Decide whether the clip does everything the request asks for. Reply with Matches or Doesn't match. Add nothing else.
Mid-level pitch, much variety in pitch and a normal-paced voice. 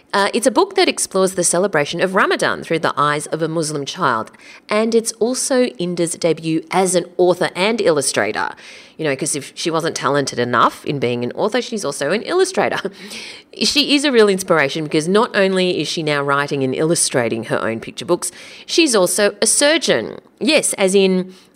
Matches